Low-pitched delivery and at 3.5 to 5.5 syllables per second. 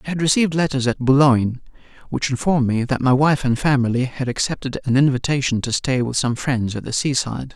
No: low, 130 Hz; 6.0 syllables/s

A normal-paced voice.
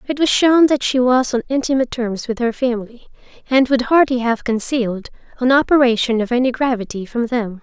Yes: average, 190 wpm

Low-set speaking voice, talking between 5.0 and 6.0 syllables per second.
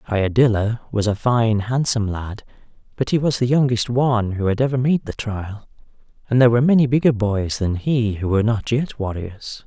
Yes: low, 115 Hz; 5.5 syllables/s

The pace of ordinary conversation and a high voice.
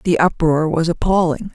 No: average, 155 wpm; medium, 165 Hz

